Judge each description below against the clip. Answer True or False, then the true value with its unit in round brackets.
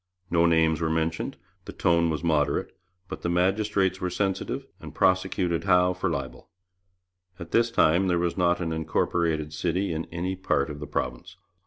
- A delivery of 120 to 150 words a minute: False (170 wpm)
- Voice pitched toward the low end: True (85 Hz)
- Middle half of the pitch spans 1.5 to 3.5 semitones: True (2.5 semitones)